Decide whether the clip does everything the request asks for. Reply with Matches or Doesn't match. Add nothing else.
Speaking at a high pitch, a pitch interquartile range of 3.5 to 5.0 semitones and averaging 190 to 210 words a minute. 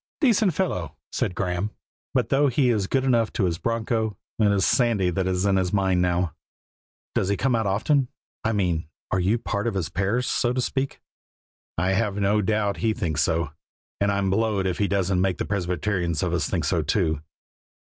Doesn't match